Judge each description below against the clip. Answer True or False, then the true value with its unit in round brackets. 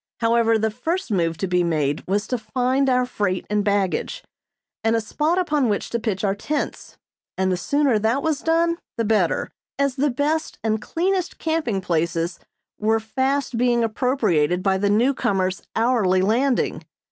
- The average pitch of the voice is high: True (225 Hz)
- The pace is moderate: True (165 wpm)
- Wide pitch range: True (5.9 semitones)